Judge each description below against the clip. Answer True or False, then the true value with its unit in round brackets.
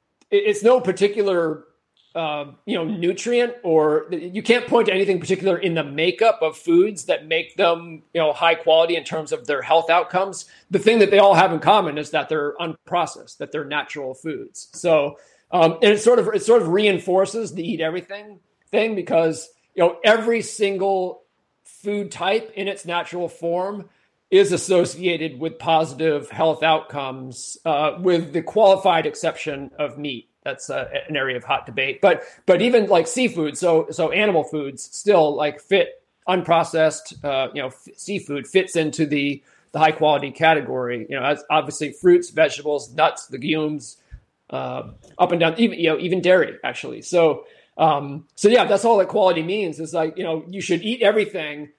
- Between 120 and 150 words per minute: False (175 wpm)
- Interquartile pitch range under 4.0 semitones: False (4.3 semitones)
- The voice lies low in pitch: False (170 Hz)